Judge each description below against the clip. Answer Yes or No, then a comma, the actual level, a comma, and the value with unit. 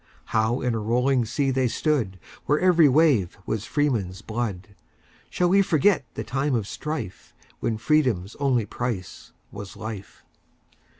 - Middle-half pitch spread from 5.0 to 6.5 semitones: Yes, wide, 5.6 semitones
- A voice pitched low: Yes, low, 120 Hz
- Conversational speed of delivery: No, slow, 125 wpm